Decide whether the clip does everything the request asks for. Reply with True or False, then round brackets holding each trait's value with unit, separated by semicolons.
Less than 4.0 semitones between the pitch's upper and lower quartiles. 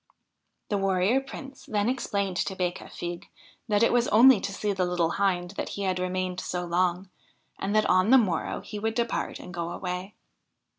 True (3.0 semitones)